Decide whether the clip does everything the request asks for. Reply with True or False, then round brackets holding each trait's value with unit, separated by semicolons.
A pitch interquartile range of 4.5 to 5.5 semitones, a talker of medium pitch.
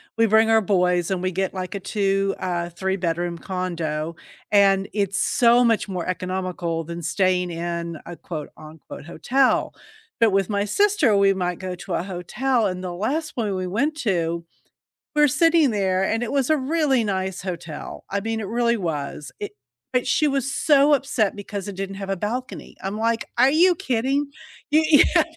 False (5.0 semitones; 195 Hz)